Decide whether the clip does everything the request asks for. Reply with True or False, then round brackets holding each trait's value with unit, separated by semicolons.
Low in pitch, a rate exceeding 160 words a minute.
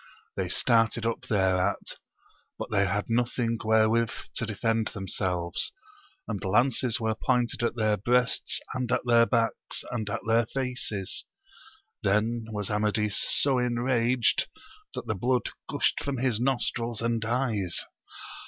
False (115 Hz; 135 wpm)